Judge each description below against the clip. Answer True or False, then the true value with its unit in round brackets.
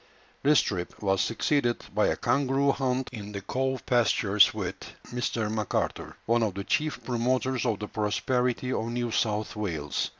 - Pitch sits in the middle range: False (120 Hz)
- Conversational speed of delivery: True (160 wpm)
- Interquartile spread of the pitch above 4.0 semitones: False (3.6 semitones)